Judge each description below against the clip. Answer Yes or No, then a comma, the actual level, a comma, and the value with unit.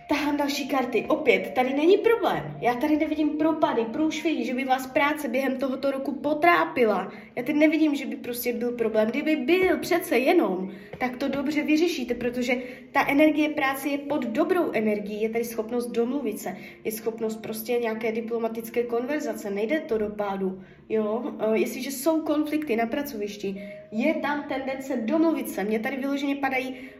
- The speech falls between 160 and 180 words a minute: Yes, average, 165 wpm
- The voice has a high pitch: Yes, very high, 260 Hz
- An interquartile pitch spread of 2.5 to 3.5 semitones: No, average, 4.9 semitones